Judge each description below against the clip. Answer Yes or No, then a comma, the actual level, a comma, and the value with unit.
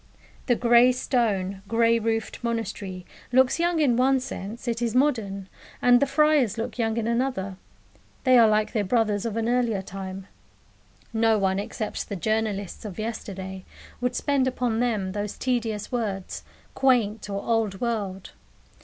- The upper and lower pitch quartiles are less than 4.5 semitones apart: Yes, average, 3.5 semitones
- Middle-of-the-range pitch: No, high, 225 Hz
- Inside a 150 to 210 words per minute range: Yes, average, 155 wpm